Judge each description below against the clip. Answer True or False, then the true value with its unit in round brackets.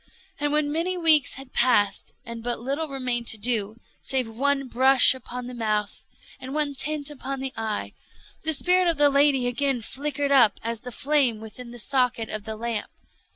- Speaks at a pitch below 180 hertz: False (260 Hz)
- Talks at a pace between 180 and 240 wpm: True (185 wpm)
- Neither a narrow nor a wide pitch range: True (3.5 semitones)